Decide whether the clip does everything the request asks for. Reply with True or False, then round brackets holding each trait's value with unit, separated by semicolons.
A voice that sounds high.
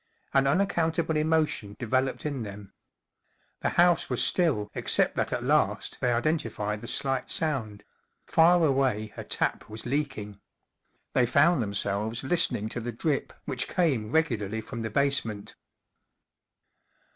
False (130 Hz)